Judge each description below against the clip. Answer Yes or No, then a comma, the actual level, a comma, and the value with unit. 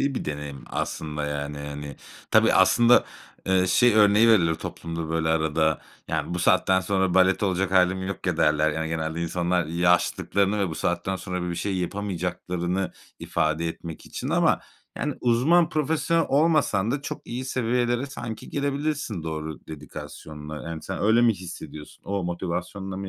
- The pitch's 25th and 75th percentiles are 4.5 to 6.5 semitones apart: Yes, average, 5.2 semitones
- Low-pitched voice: Yes, very low, 90 Hz